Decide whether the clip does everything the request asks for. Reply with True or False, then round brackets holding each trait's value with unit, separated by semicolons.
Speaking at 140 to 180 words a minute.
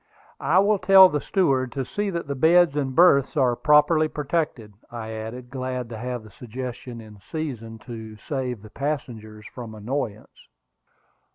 True (160 wpm)